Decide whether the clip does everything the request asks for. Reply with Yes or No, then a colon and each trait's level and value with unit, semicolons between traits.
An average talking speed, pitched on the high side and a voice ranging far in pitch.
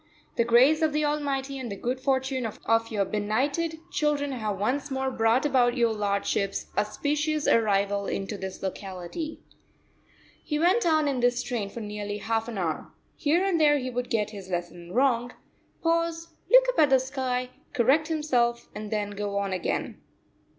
Yes: average, 170 wpm; high, 245 Hz; wide, 5.9 semitones